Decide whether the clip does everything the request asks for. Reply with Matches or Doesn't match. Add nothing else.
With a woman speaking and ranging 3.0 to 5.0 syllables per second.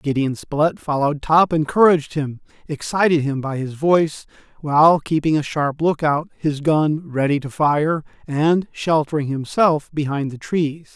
Doesn't match